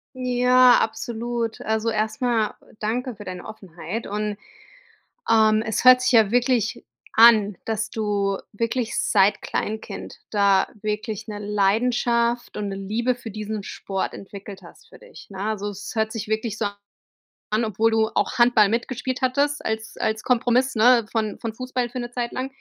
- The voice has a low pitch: No, high, 220 Hz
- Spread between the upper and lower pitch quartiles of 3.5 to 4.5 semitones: No, narrow, 2.5 semitones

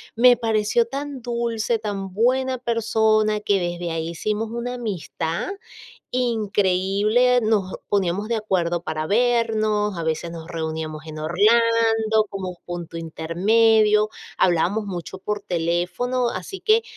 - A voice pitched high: Yes, high, 210 Hz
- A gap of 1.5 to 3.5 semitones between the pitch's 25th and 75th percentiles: No, average, 4.8 semitones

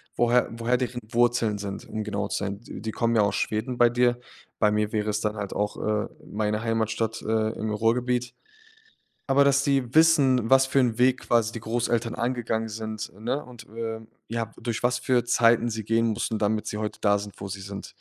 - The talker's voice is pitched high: No, low, 115 Hz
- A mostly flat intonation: Yes, narrow, 2.3 semitones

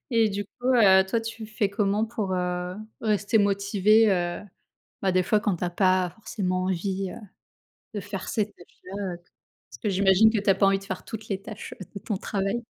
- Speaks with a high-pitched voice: Yes, high, 200 Hz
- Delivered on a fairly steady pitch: Yes, narrow, 2.3 semitones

